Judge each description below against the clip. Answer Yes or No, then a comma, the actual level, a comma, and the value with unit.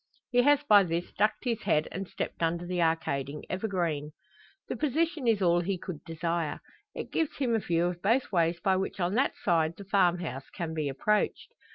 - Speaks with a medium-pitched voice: Yes, medium, 180 Hz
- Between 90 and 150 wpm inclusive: No, average, 195 wpm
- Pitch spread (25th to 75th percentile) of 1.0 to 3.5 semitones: No, average, 4.3 semitones